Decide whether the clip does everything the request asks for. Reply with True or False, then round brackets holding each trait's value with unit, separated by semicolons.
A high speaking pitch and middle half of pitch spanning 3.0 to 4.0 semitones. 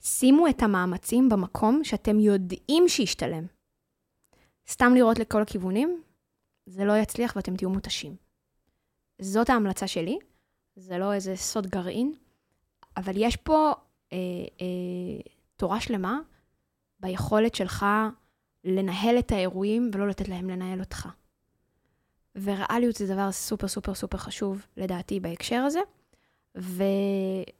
True (200 Hz; 3.7 semitones)